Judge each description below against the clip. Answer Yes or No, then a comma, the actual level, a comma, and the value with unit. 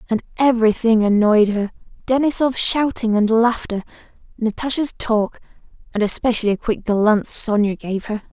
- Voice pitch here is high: Yes, high, 225 Hz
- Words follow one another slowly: Yes, slow, 120 wpm